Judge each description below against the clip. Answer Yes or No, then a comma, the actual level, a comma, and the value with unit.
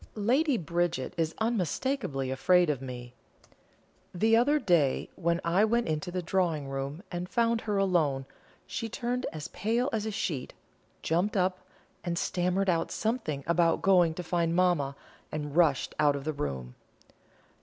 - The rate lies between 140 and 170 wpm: Yes, average, 155 wpm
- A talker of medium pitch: Yes, medium, 175 Hz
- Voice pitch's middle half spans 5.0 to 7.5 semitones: Yes, wide, 5.6 semitones